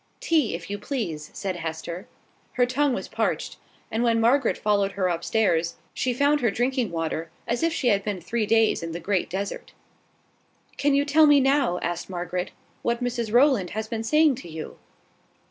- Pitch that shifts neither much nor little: No, wide, 6.4 semitones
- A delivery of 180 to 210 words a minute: Yes, average, 190 wpm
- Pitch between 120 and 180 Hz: No, high, 220 Hz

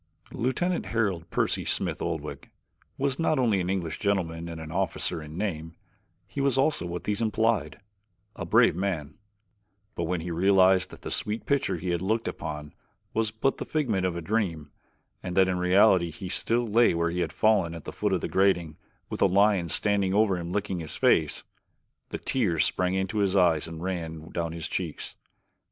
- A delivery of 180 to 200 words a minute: Yes, average, 190 wpm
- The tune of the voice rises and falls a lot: No, average, 4.1 semitones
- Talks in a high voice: No, very low, 95 Hz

